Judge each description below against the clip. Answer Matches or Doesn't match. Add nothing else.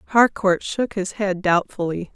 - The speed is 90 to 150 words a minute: Matches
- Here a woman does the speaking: Matches